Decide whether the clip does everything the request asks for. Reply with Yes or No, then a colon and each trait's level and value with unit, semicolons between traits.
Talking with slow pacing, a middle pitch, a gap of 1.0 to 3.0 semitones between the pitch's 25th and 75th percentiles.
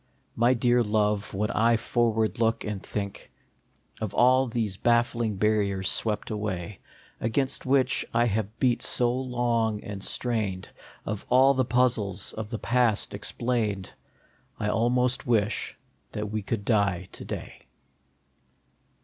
No: slow, 130 wpm; low, 110 Hz; average, 2.7 semitones